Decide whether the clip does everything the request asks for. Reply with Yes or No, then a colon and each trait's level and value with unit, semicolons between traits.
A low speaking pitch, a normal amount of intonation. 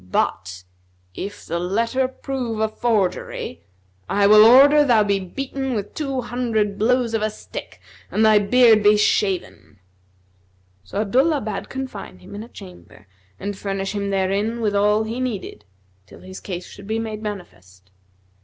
No: high, 210 Hz; average, 3.3 semitones